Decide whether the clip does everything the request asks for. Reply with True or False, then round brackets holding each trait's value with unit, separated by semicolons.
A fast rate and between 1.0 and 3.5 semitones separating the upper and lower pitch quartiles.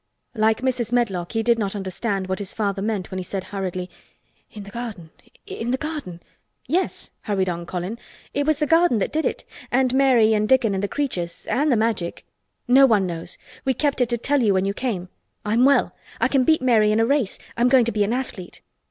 False (215 wpm; 4.9 semitones)